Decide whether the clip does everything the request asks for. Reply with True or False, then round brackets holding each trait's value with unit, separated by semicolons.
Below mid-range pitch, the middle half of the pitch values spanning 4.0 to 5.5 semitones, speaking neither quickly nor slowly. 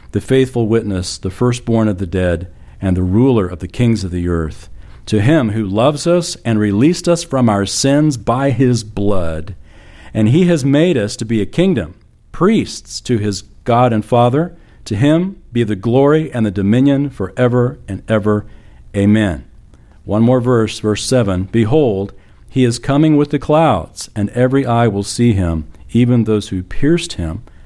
True (110 Hz; 4.9 semitones; 180 wpm)